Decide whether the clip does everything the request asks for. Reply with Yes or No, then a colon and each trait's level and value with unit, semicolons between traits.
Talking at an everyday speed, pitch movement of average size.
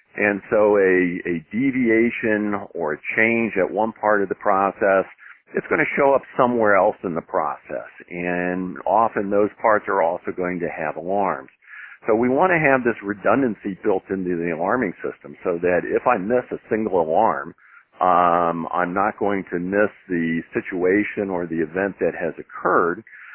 Yes: average, 175 wpm; average, 3.8 semitones